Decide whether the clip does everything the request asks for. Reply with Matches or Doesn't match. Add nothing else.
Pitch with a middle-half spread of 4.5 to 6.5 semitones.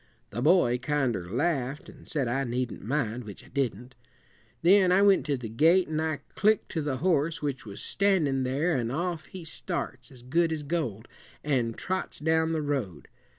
Matches